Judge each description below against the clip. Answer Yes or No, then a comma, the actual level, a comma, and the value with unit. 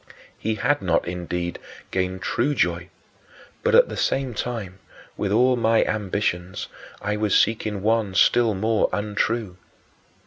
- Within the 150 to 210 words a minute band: No, slow, 135 wpm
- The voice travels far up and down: No, average, 3.6 semitones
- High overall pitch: No, low, 105 Hz